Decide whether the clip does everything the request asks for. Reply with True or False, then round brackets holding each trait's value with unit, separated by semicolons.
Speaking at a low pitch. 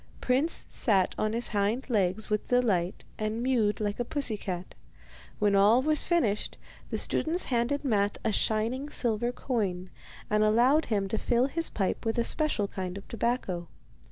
False (220 Hz)